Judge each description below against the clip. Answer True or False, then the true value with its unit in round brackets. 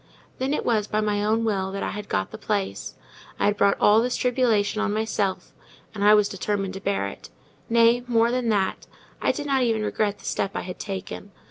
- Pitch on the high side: True (210 Hz)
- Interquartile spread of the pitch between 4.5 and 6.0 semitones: False (2.4 semitones)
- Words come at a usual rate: False (220 wpm)